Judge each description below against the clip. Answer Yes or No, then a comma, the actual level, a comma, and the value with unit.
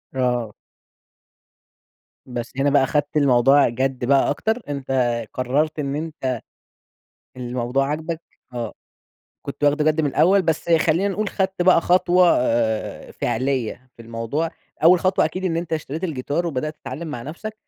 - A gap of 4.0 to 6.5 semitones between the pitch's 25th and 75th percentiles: Yes, average, 4.5 semitones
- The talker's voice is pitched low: No, medium, 145 Hz